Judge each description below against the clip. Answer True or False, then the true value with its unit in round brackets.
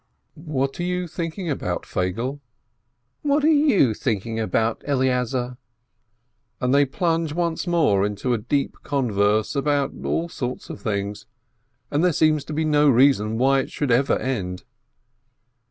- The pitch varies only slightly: False (5.6 semitones)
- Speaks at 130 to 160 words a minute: True (155 wpm)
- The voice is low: True (130 Hz)